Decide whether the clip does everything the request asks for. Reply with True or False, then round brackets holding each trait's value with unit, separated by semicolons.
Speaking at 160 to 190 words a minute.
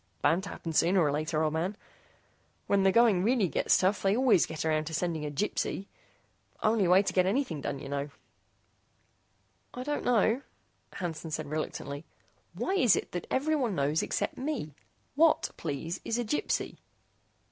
True (170 wpm)